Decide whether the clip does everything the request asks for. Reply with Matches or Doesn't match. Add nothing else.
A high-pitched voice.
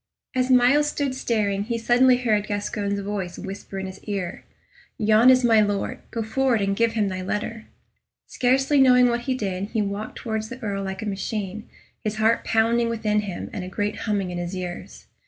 Matches